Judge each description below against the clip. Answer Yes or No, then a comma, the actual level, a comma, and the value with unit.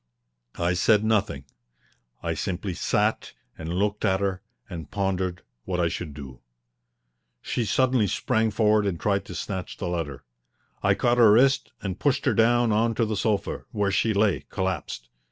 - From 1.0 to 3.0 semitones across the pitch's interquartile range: No, average, 3.8 semitones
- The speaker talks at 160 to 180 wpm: Yes, average, 165 wpm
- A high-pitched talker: No, low, 100 Hz